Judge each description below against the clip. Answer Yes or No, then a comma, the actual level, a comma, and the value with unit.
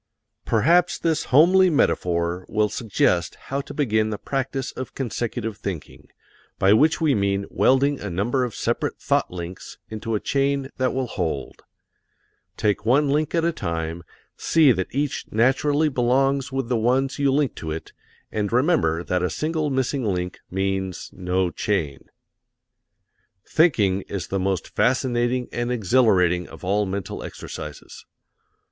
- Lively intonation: Yes, wide, 6.2 semitones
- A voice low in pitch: Yes, low, 120 Hz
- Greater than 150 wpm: No, average, 145 wpm